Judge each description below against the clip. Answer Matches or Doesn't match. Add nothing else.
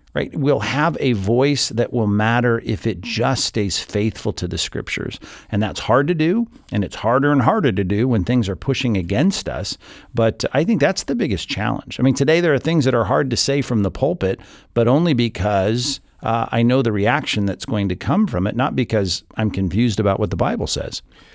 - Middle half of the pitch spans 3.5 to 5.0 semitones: Matches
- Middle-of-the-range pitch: Doesn't match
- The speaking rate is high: Matches